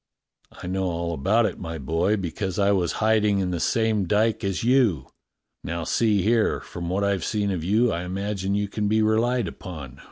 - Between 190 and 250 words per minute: Yes, average, 195 wpm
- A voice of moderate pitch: No, low, 100 Hz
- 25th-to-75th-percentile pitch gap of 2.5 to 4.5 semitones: Yes, average, 3.8 semitones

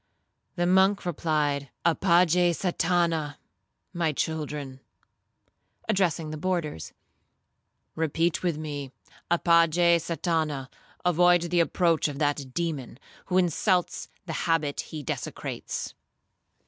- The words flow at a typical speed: No, slow, 95 wpm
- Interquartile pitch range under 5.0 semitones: Yes, average, 2.7 semitones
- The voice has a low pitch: No, medium, 165 Hz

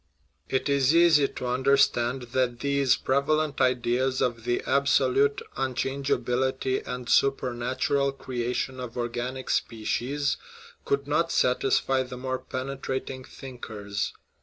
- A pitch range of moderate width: No, narrow, 1.8 semitones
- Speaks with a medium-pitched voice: No, low, 130 Hz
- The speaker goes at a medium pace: No, slow, 115 wpm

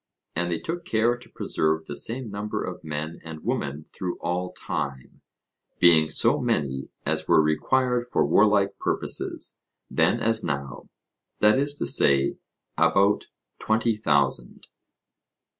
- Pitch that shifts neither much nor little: No, wide, 6.3 semitones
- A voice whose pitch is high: No, very low, 90 Hz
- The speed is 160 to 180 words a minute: No, slow, 135 wpm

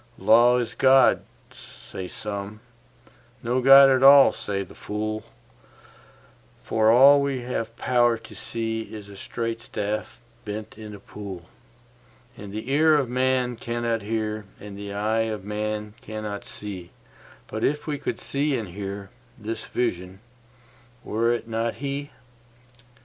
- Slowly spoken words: Yes, slow, 130 wpm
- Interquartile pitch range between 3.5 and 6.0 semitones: No, average, 2.8 semitones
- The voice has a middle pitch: No, low, 115 Hz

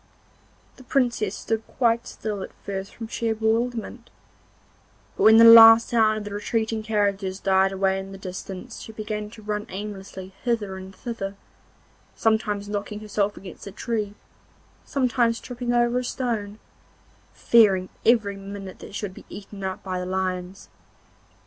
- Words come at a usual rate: Yes, average, 155 wpm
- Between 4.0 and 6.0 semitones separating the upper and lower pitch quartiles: No, average, 2.8 semitones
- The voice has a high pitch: Yes, high, 210 Hz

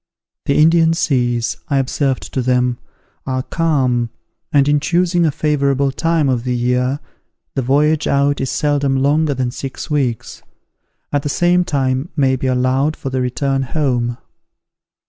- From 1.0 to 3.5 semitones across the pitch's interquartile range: Yes, average, 2.8 semitones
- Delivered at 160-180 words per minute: No, average, 150 wpm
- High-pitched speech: No, low, 135 Hz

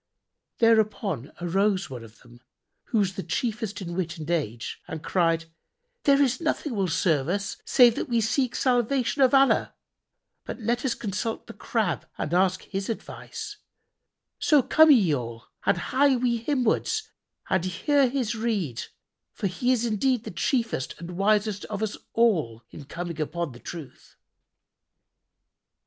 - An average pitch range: No, wide, 6.1 semitones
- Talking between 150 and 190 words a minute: Yes, average, 155 wpm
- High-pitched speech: Yes, high, 205 Hz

